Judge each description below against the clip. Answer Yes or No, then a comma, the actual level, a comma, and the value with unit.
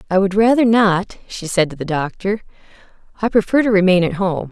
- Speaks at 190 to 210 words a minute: Yes, average, 200 wpm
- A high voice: Yes, high, 195 Hz